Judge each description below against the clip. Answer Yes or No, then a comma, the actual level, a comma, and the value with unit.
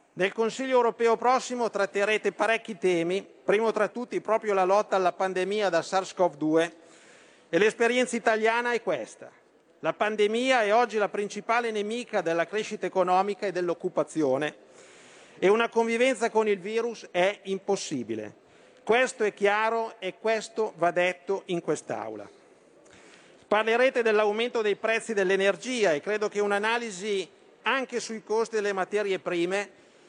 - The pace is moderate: Yes, average, 130 wpm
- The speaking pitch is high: Yes, high, 210 Hz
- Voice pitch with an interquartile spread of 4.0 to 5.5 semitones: No, average, 3.1 semitones